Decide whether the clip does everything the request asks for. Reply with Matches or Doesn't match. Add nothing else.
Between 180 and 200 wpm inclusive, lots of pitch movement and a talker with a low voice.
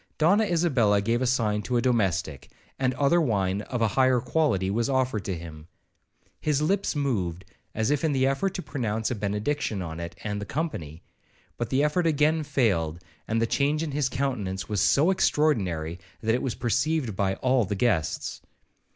Matches